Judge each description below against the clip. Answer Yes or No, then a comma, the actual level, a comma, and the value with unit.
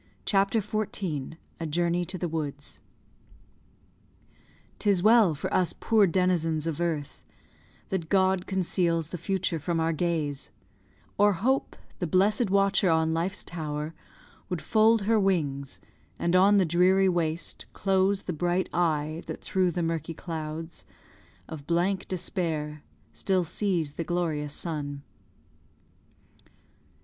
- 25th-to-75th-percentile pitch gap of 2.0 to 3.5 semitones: Yes, average, 3.1 semitones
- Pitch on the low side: No, medium, 175 Hz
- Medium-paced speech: No, slow, 125 wpm